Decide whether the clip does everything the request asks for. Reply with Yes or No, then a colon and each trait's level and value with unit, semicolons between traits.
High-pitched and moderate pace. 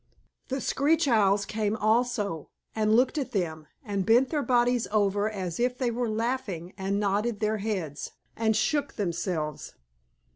Yes: high, 215 Hz; average, 150 wpm